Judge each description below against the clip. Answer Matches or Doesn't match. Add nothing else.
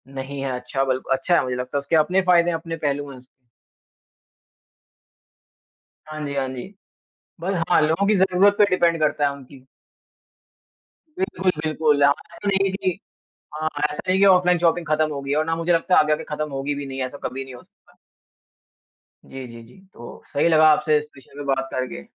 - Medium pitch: Matches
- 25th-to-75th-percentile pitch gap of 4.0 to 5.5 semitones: Matches